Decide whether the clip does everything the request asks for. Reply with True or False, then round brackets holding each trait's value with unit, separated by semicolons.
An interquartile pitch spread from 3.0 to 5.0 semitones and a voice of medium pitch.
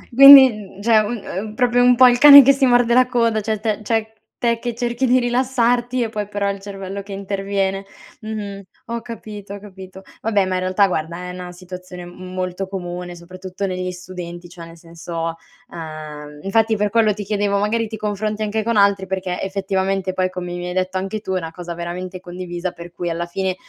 False (3.4 semitones; 195 Hz)